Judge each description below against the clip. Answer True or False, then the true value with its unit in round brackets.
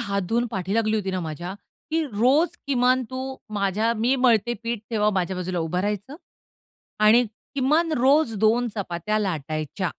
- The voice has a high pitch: True (215 Hz)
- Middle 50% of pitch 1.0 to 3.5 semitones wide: False (4.7 semitones)